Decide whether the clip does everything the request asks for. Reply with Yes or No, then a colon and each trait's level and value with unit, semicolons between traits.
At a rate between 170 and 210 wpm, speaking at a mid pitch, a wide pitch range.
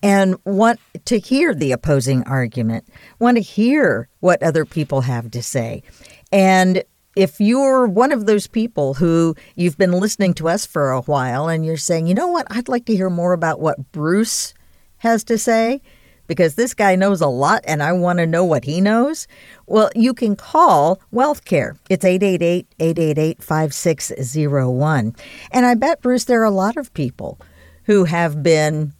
Yes: average, 175 wpm; medium, 180 Hz; wide, 6.3 semitones